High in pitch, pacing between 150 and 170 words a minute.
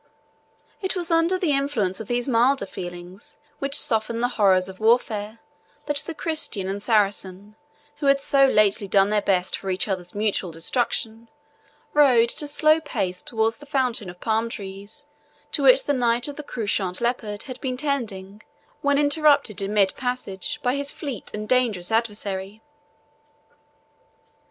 Yes: high, 225 Hz; average, 160 wpm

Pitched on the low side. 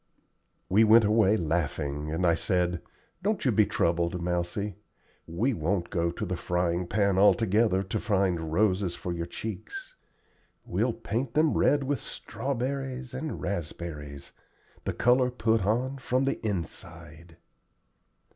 Yes: very low, 95 Hz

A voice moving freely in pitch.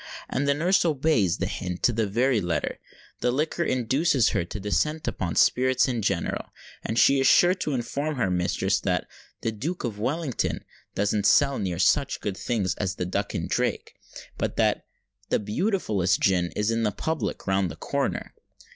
Yes: wide, 6.3 semitones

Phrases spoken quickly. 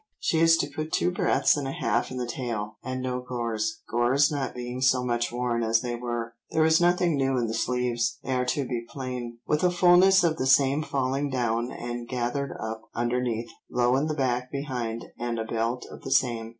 Yes: fast, 210 wpm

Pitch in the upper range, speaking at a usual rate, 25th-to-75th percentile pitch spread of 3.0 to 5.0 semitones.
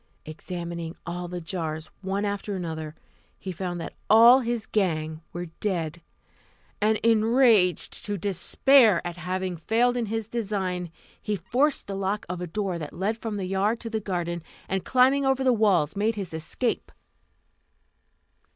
Yes: high, 195 Hz; average, 155 wpm; average, 4.3 semitones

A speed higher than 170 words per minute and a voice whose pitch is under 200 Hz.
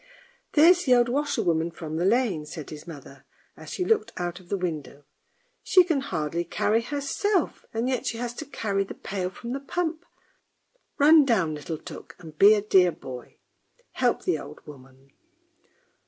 No: average, 180 wpm; high, 205 Hz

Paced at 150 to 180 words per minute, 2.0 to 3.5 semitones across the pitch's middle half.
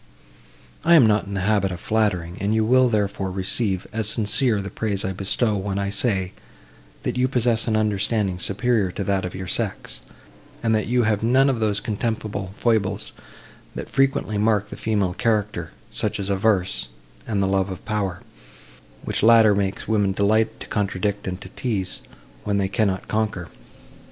Yes: average, 170 wpm; narrow, 2.4 semitones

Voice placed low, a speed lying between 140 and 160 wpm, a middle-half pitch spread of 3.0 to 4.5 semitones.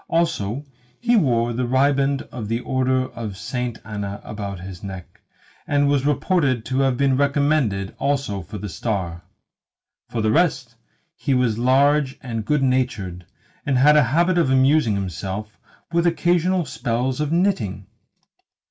No: low, 130 Hz; average, 150 wpm; average, 5.1 semitones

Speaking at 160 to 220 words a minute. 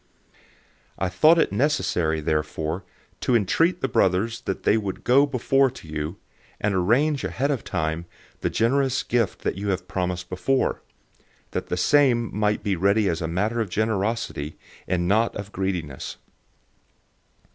No: average, 150 wpm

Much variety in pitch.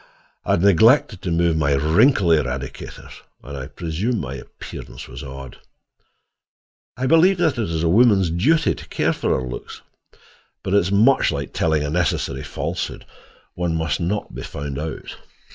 Yes: wide, 6.7 semitones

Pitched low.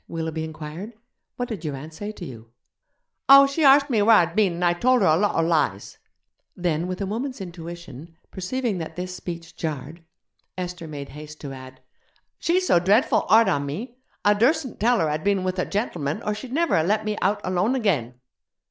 No: medium, 180 Hz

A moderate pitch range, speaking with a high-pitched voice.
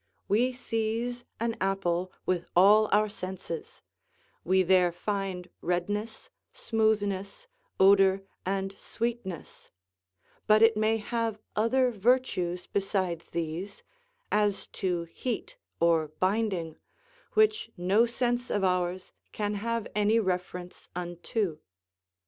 Yes: average, 3.7 semitones; high, 200 Hz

